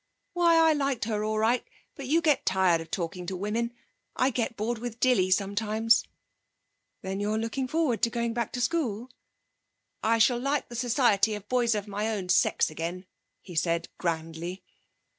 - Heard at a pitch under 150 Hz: No, high, 220 Hz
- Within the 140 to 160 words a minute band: No, average, 175 wpm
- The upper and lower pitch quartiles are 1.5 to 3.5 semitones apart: No, average, 4.4 semitones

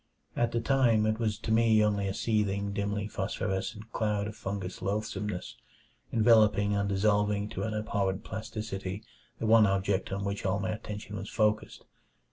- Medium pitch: No, low, 105 Hz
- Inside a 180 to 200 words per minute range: No, average, 160 wpm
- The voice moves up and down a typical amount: No, narrow, 1.5 semitones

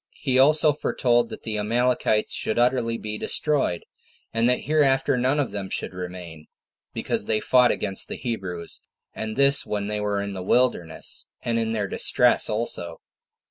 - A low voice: Yes, low, 115 Hz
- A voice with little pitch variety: No, average, 4.0 semitones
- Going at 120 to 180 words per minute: Yes, average, 165 wpm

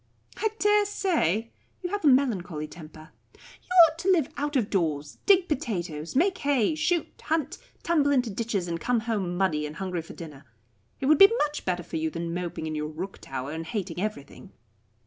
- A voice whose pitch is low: No, high, 200 Hz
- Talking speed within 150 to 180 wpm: No, average, 190 wpm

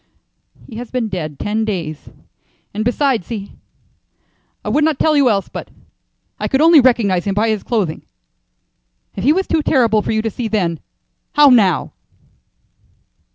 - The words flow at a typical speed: Yes, average, 160 wpm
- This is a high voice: Yes, high, 220 Hz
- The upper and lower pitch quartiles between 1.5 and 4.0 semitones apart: No, average, 4.7 semitones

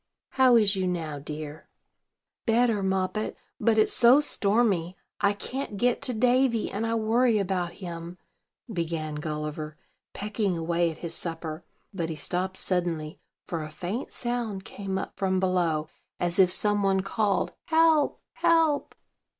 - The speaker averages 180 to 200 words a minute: No, average, 145 wpm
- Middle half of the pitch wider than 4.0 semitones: Yes, average, 5.1 semitones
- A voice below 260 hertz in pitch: Yes, high, 190 Hz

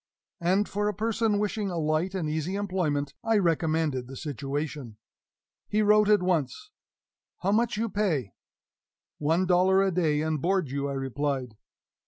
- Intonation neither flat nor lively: No, wide, 5.7 semitones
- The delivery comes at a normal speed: Yes, average, 155 wpm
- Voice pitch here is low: No, medium, 175 Hz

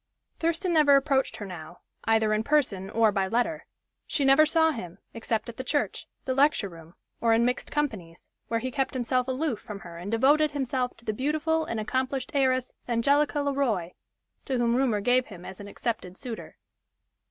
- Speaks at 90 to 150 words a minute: No, average, 185 wpm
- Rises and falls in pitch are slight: No, average, 4.7 semitones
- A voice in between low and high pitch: No, very high, 250 Hz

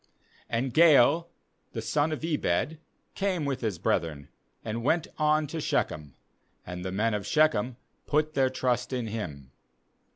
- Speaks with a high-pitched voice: No, low, 130 Hz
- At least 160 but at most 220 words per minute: No, average, 150 wpm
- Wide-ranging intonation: Yes, wide, 6.8 semitones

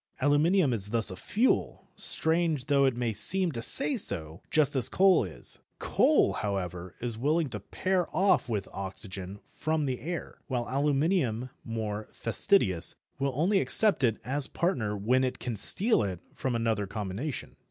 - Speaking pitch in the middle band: No, low, 125 Hz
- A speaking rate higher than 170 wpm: No, average, 160 wpm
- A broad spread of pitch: Yes, wide, 7.3 semitones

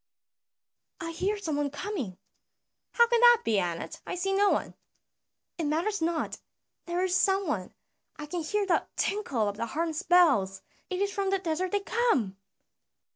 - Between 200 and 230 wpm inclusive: No, average, 170 wpm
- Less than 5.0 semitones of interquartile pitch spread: No, wide, 5.5 semitones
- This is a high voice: Yes, very high, 345 Hz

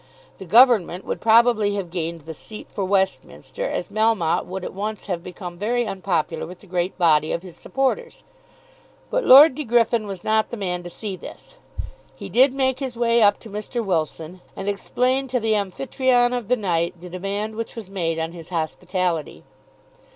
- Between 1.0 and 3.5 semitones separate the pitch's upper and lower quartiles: No, average, 5.0 semitones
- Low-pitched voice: No, high, 200 Hz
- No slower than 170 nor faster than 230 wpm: Yes, average, 185 wpm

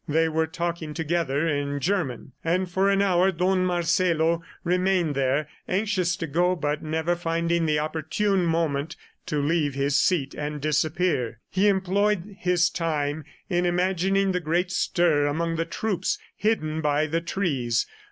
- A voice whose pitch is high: No, medium, 165 Hz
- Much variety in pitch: No, average, 3.2 semitones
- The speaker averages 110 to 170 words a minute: Yes, average, 150 wpm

